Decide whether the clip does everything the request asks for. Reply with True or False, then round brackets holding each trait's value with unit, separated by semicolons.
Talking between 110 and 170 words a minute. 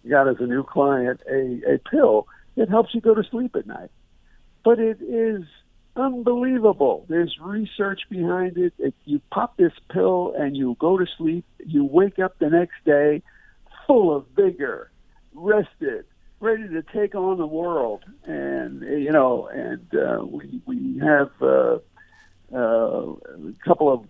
True (160 wpm)